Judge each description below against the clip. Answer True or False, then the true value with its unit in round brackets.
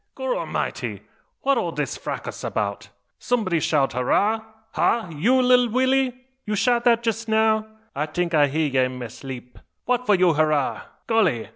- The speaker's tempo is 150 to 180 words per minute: True (160 wpm)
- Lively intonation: True (8.6 semitones)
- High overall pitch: True (205 Hz)